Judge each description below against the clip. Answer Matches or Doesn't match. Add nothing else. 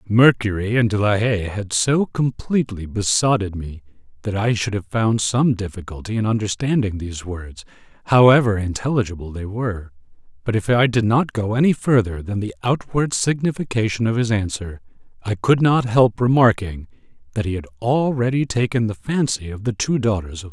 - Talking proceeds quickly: Doesn't match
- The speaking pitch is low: Matches